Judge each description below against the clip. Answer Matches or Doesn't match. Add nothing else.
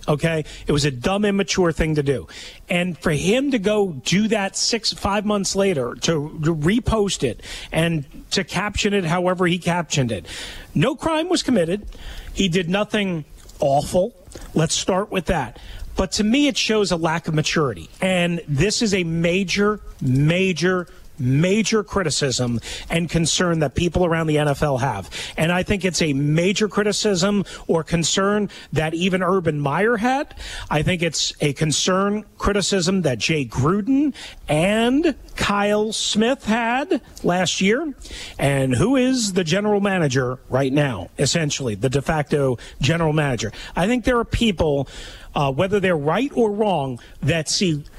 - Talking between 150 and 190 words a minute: Matches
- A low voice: Doesn't match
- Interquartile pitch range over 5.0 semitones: Matches